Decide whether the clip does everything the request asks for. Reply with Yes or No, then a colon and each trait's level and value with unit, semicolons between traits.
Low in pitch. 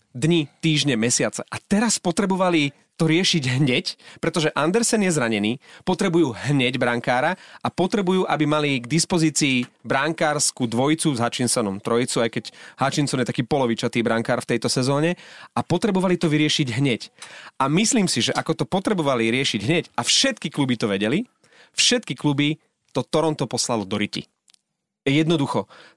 No: medium, 150 Hz